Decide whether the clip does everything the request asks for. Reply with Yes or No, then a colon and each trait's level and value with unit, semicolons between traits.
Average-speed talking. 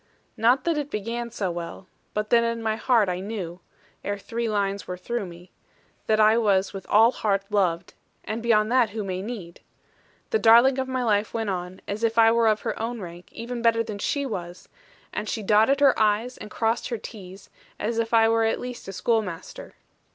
No: fast, 210 wpm